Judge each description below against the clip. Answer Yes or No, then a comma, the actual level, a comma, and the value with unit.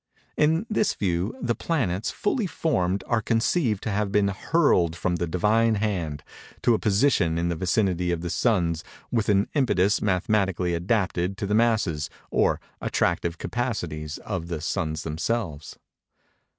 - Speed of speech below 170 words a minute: Yes, average, 150 wpm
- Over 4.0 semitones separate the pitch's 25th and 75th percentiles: Yes, average, 4.8 semitones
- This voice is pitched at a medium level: No, very low, 95 Hz